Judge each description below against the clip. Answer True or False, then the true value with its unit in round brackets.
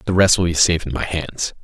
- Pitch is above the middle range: False (85 Hz)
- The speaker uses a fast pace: True (295 wpm)